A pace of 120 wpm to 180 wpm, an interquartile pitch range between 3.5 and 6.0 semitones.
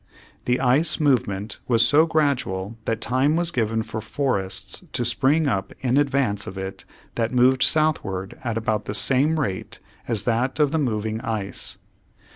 Yes: average, 160 wpm; average, 4.9 semitones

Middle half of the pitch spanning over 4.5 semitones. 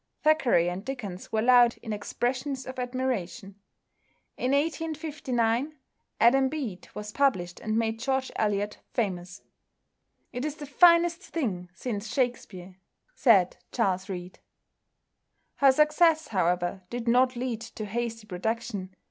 Yes: average, 5.1 semitones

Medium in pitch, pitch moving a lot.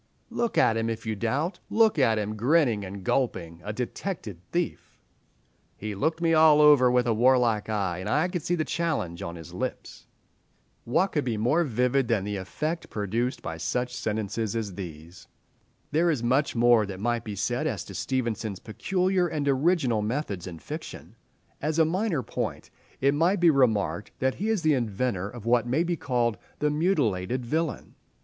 No: low, 125 Hz; wide, 6.6 semitones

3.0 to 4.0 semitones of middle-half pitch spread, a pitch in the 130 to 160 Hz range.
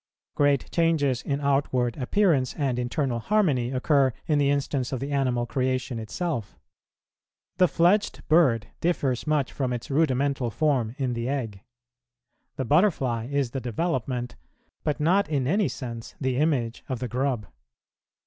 Yes: average, 3.4 semitones; low, 135 Hz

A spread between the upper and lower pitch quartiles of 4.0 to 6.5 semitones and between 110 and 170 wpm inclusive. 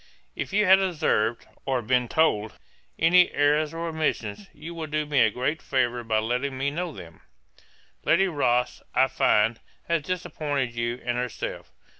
Yes: average, 5.1 semitones; average, 160 wpm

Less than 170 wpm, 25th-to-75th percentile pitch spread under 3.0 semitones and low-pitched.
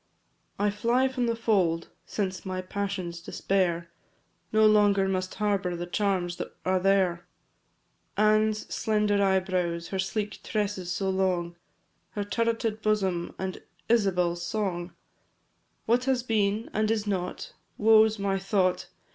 No: slow, 135 wpm; narrow, 2.6 semitones; high, 195 Hz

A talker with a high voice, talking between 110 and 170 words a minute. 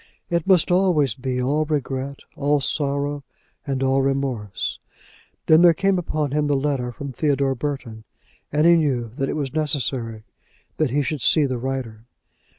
No: medium, 140 Hz; average, 160 wpm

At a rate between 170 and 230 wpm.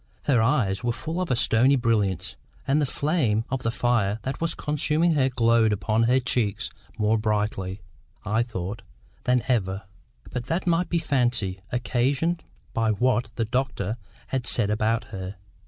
No: average, 160 wpm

